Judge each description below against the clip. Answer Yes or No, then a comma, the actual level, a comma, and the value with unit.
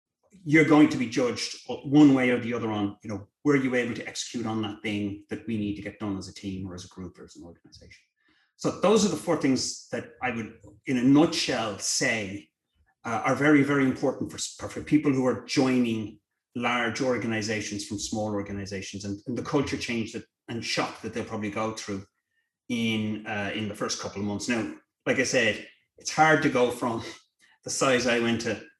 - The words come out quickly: Yes, fast, 215 wpm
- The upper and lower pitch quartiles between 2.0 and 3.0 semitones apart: No, average, 4.3 semitones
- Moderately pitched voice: No, low, 115 Hz